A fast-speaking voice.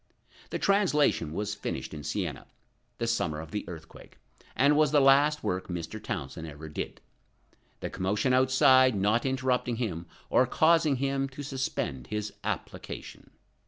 No: average, 145 wpm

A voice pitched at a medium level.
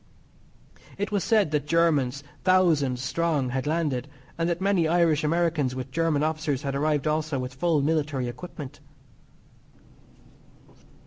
Yes: medium, 155 Hz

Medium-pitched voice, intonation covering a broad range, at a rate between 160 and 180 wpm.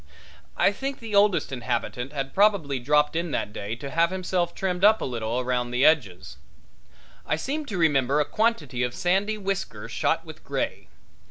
Yes: medium, 150 Hz; wide, 7.8 semitones; average, 175 wpm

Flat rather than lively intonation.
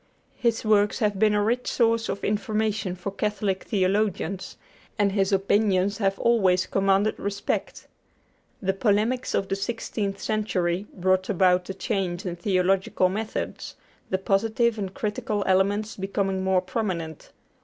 Yes: narrow, 2.1 semitones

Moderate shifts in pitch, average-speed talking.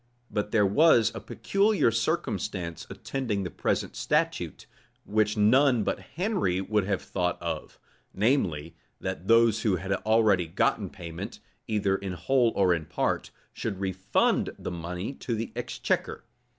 Yes: average, 3.8 semitones; average, 145 wpm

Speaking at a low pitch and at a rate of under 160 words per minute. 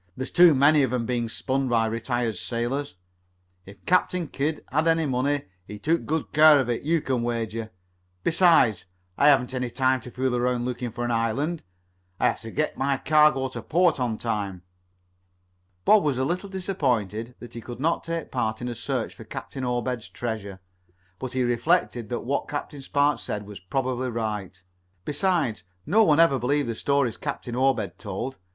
No: low, 130 Hz; average, 180 wpm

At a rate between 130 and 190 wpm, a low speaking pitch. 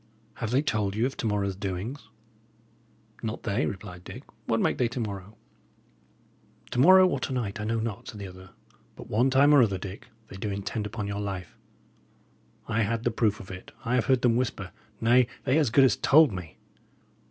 No: average, 200 wpm; low, 110 Hz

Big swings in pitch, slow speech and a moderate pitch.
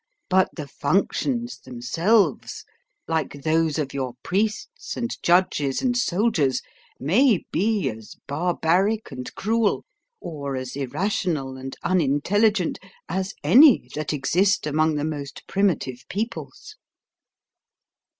Yes: wide, 6.4 semitones; slow, 110 wpm; medium, 165 Hz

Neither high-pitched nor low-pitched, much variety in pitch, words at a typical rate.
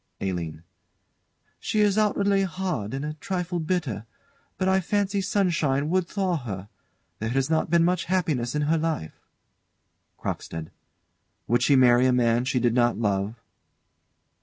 Yes: medium, 150 Hz; wide, 7.6 semitones; average, 145 wpm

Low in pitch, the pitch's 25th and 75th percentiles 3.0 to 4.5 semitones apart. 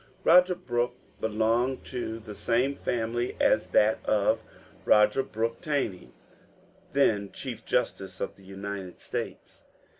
Yes: low, 115 Hz; average, 3.6 semitones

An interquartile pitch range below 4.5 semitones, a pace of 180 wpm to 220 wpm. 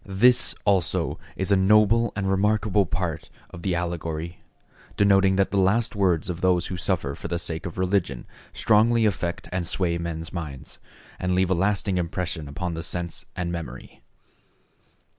No: average, 2.7 semitones; average, 160 wpm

